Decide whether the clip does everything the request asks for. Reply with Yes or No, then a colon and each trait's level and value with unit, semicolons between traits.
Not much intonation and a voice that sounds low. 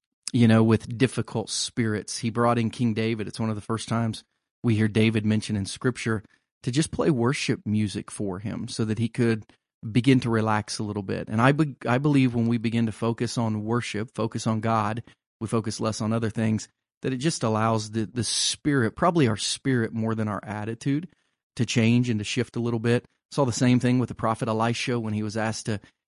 Yes: narrow, 2.0 semitones; low, 115 Hz